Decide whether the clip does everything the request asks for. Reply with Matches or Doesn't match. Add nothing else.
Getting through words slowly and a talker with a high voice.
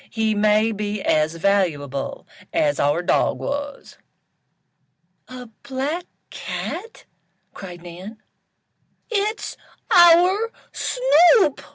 Matches